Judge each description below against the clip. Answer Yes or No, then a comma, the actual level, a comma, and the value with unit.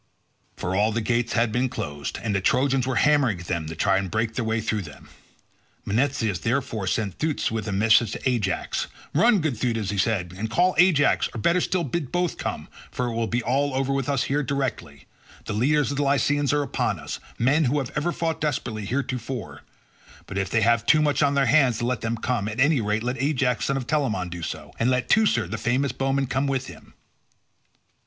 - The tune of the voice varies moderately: Yes, average, 4.4 semitones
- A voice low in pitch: Yes, low, 125 Hz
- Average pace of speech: No, fast, 220 wpm